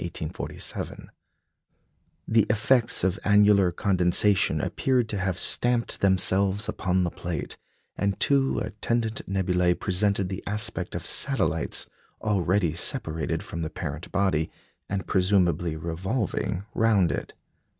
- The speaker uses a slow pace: Yes, slow, 110 wpm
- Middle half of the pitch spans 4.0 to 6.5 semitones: No, average, 3.2 semitones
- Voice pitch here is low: Yes, very low, 95 Hz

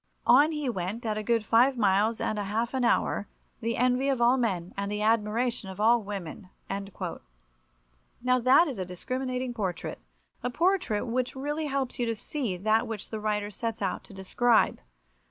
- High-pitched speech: Yes, high, 230 Hz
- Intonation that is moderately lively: Yes, average, 3.5 semitones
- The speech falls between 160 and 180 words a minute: Yes, average, 175 wpm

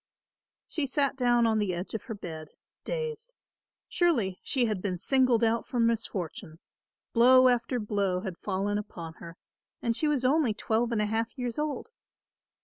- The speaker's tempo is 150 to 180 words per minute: Yes, average, 165 wpm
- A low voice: No, high, 230 Hz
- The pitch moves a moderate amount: Yes, average, 4.3 semitones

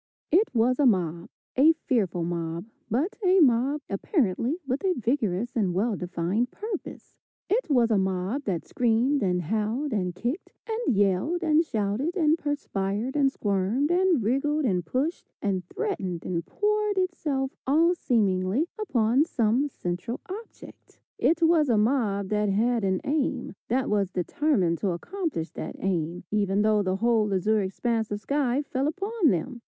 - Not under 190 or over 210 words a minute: No, average, 155 wpm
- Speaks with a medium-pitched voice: No, high, 235 Hz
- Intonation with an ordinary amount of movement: No, wide, 7.3 semitones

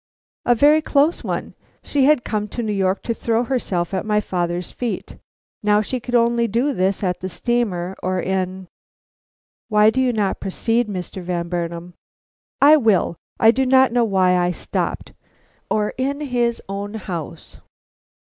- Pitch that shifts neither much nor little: Yes, average, 4.7 semitones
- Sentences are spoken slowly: No, average, 165 wpm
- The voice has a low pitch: No, high, 210 Hz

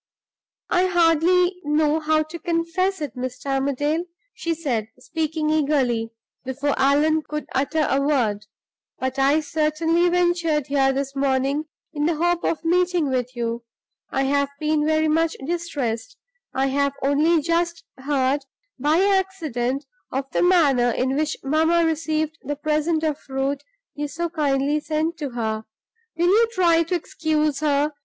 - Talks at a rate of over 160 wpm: No, average, 150 wpm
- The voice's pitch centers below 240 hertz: No, very high, 305 Hz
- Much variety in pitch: No, average, 3.4 semitones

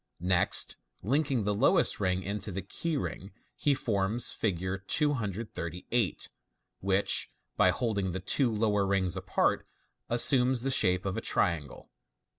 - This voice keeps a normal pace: No, slow, 130 wpm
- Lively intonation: No, average, 4.4 semitones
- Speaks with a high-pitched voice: No, low, 105 Hz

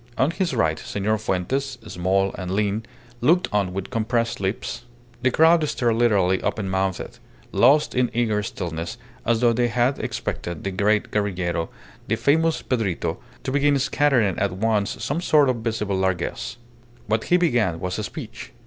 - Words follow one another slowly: No, average, 160 wpm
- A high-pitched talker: No, low, 110 Hz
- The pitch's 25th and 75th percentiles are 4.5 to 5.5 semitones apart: Yes, average, 5.0 semitones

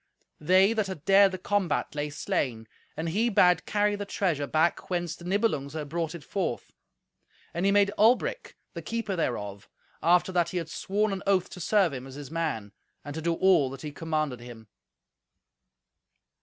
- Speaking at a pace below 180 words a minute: No, average, 185 wpm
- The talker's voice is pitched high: No, medium, 170 Hz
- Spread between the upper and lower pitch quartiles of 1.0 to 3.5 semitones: No, average, 4.9 semitones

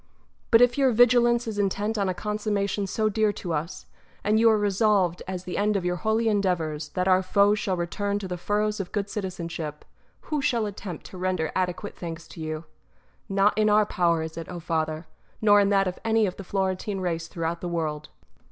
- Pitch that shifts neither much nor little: Yes, average, 3.5 semitones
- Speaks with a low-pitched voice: No, high, 195 Hz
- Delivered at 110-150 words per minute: No, fast, 205 wpm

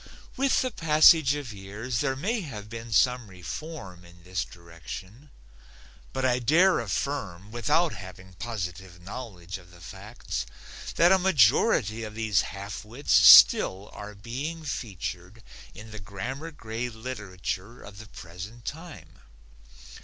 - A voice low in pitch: Yes, low, 110 Hz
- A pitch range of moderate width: No, wide, 6.4 semitones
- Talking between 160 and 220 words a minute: No, slow, 135 wpm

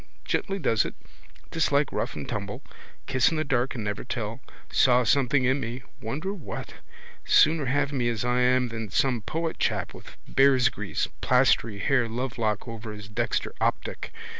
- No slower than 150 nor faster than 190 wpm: Yes, average, 165 wpm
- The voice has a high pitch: No, low, 125 Hz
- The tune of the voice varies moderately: Yes, average, 3.3 semitones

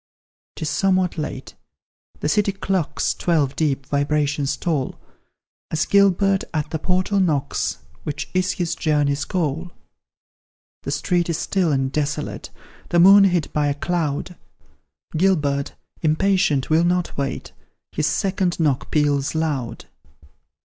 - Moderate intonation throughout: Yes, average, 4.1 semitones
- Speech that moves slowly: Yes, slow, 125 wpm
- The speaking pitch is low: No, medium, 155 Hz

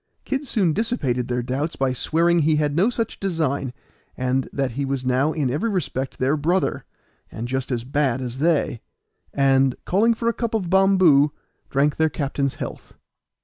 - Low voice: No, medium, 145 Hz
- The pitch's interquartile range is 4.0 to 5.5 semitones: Yes, average, 5.1 semitones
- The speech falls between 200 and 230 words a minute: No, average, 175 wpm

